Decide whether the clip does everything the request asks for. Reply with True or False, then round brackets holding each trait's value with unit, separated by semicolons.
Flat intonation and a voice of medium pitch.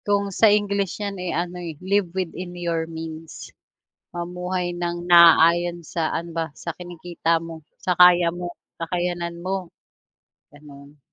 True (1.3 semitones; 175 Hz)